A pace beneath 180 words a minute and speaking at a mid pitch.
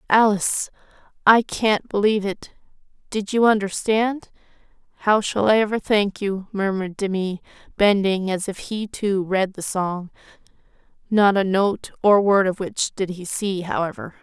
No: average, 140 wpm; high, 200 Hz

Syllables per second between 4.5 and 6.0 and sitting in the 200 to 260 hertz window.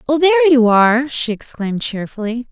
Yes: 5.5 syllables/s; high, 240 Hz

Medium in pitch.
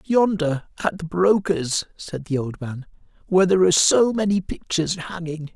Yes: medium, 170 Hz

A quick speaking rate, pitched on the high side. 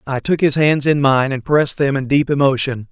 No: fast, 245 wpm; medium, 140 Hz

